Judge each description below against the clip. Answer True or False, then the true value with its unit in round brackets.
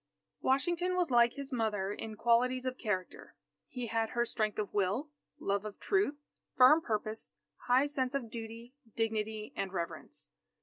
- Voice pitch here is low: False (235 Hz)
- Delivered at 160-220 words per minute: False (150 wpm)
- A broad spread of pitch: False (3.4 semitones)